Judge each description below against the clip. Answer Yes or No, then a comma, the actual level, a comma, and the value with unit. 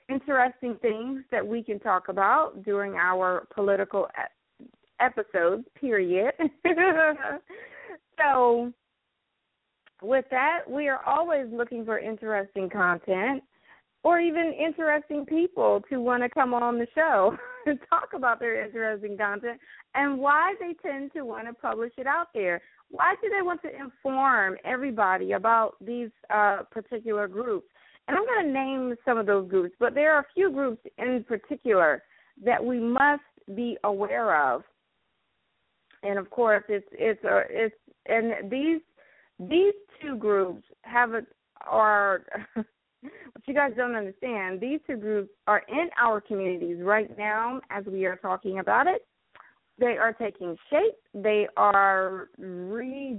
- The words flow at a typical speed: Yes, average, 145 wpm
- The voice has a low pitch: No, high, 240 Hz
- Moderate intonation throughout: No, wide, 5.8 semitones